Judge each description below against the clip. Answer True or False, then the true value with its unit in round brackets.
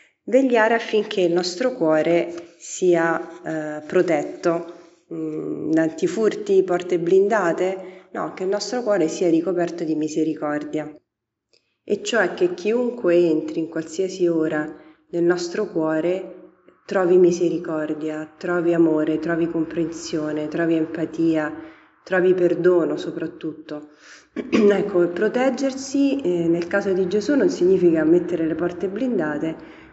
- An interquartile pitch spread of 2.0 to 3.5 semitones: True (3.2 semitones)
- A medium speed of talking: False (110 wpm)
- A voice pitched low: False (175 Hz)